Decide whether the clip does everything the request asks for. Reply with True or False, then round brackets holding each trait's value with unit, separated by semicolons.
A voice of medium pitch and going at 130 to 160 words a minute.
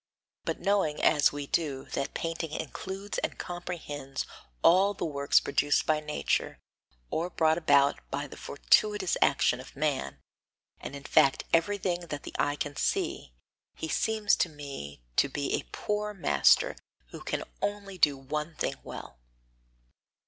True (155 Hz; 150 wpm)